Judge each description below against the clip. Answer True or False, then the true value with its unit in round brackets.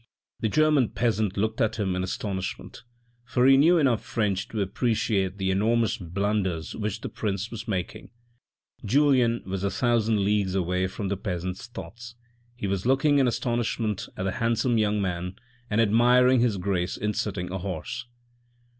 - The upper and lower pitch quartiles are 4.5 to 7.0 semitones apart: False (3.7 semitones)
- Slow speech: False (165 wpm)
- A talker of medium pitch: False (105 Hz)